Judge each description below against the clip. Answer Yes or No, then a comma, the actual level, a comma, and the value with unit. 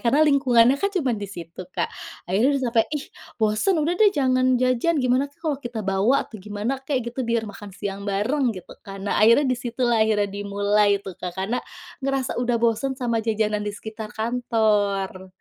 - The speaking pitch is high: Yes, high, 230 Hz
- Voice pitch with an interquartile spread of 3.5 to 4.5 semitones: Yes, average, 3.8 semitones